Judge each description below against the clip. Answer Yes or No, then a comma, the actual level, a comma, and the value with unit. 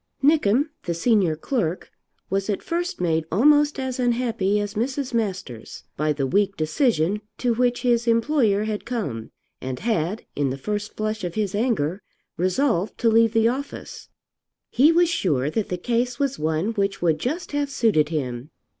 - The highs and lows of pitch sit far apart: Yes, wide, 6.4 semitones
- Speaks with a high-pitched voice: Yes, high, 215 Hz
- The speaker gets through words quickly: No, average, 165 wpm